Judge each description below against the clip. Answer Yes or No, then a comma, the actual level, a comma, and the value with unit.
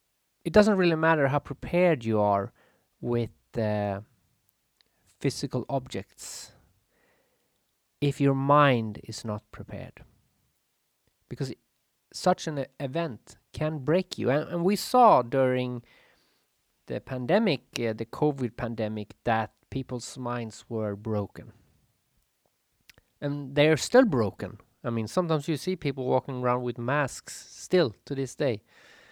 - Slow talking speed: Yes, slow, 130 wpm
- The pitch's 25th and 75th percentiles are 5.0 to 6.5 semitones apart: Yes, average, 5.3 semitones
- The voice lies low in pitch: Yes, low, 130 Hz